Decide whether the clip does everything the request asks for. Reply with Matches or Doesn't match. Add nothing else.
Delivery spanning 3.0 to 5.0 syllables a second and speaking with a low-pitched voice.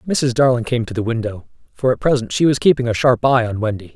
Doesn't match